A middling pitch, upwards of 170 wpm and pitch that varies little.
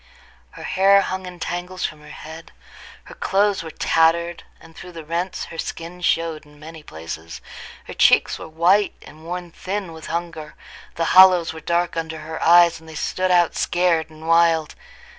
Yes: medium, 165 Hz; average, 180 wpm; narrow, 1.9 semitones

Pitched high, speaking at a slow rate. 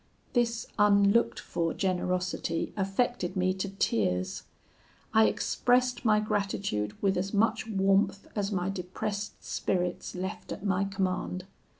Yes: high, 195 Hz; slow, 120 wpm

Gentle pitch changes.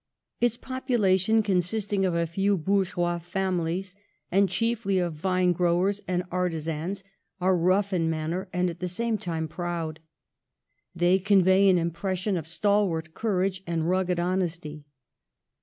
Yes: narrow, 2.3 semitones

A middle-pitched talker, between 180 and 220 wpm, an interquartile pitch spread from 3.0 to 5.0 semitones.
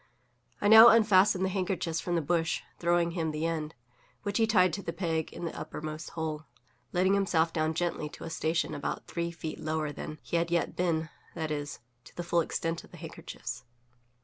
No: medium, 170 Hz; average, 200 wpm; narrow, 2.4 semitones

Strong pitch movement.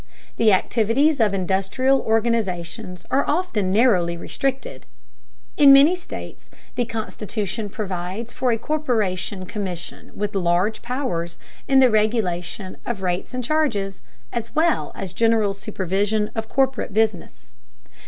No: average, 4.6 semitones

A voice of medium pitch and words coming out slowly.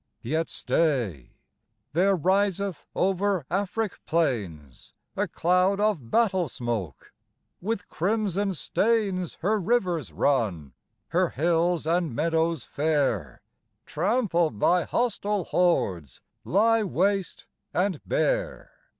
Yes: medium, 175 Hz; slow, 100 wpm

